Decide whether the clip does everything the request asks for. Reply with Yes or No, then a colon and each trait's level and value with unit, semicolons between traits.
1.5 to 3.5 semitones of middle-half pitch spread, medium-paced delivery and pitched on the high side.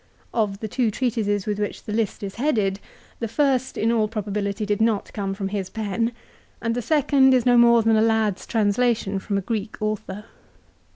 Yes: narrow, 2.5 semitones; average, 190 wpm; high, 215 Hz